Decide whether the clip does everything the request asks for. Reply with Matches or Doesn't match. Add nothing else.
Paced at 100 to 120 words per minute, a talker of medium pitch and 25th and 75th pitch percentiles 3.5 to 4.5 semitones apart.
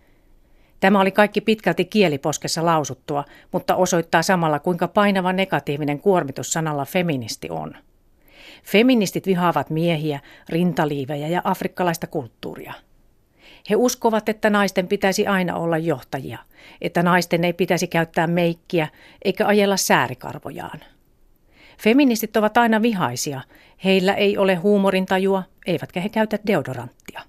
Matches